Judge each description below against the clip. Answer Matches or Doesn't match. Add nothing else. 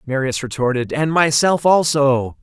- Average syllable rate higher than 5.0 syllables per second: Doesn't match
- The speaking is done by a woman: Doesn't match